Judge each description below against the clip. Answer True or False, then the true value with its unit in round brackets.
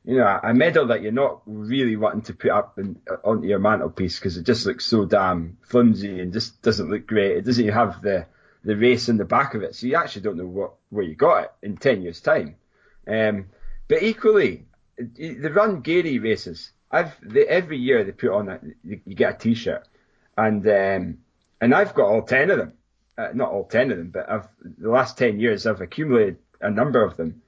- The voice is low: True (110 Hz)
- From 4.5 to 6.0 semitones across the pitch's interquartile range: False (3.9 semitones)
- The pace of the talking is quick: True (215 wpm)